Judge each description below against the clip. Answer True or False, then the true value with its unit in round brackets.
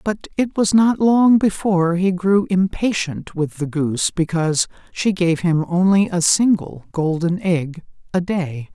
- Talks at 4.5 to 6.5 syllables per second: False (4.3 syllables/s)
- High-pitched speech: False (180 Hz)